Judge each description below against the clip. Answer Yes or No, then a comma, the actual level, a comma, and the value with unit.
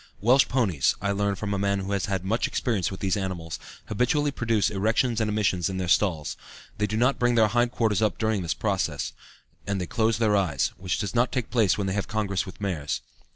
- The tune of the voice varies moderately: Yes, average, 3.0 semitones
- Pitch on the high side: No, low, 100 Hz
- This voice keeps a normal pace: No, fast, 225 wpm